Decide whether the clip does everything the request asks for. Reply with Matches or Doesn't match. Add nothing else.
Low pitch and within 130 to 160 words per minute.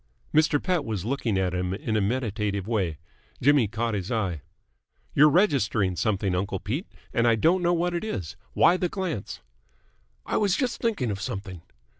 Doesn't match